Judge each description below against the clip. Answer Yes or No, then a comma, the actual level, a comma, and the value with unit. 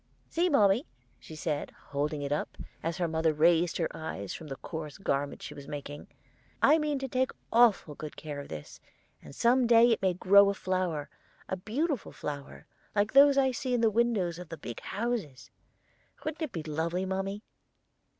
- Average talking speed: Yes, average, 185 wpm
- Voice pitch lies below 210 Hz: Yes, medium, 185 Hz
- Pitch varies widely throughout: Yes, wide, 7.6 semitones